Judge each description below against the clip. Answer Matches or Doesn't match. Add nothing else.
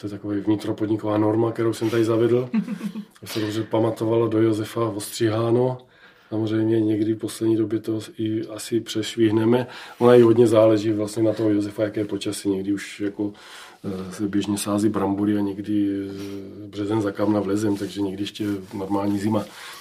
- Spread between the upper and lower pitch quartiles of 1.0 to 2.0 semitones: Matches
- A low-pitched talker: Matches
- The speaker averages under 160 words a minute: Doesn't match